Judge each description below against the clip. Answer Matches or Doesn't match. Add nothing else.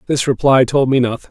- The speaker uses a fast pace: Matches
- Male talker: Matches